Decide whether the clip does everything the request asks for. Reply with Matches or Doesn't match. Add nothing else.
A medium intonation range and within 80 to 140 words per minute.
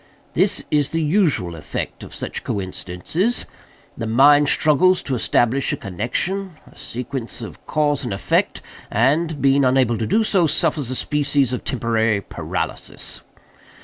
Matches